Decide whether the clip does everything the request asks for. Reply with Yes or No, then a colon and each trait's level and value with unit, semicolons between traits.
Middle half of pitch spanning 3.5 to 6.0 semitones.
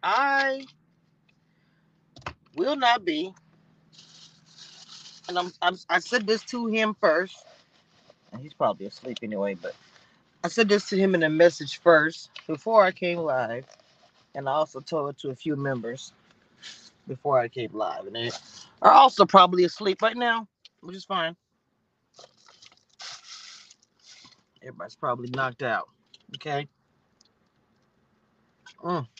Yes: average, 4.2 semitones